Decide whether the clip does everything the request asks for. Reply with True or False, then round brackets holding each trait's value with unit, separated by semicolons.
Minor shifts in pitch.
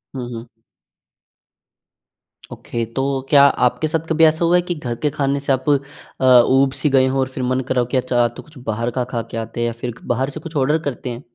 False (3.0 semitones)